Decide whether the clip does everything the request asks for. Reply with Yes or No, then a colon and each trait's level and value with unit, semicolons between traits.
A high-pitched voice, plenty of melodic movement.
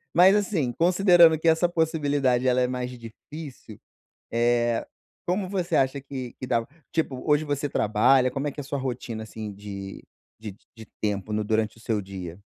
No: low, 130 Hz; wide, 5.8 semitones